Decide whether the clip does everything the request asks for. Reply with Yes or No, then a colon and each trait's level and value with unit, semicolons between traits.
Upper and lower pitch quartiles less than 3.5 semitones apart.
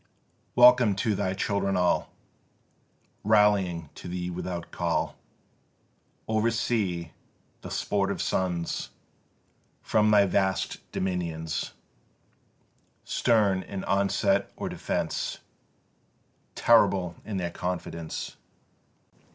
Yes: average, 2.7 semitones